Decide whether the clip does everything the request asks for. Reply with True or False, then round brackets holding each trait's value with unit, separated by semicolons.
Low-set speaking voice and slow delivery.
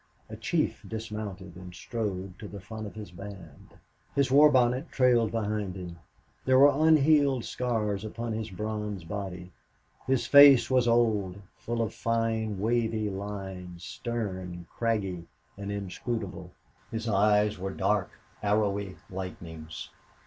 True (105 Hz; 130 wpm)